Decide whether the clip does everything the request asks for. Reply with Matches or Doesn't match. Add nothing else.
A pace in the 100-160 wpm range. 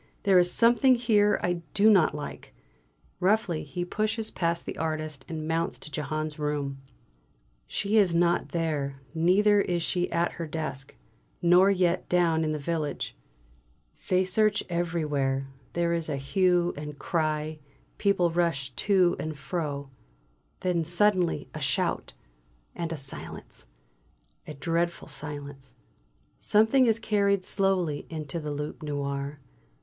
Matches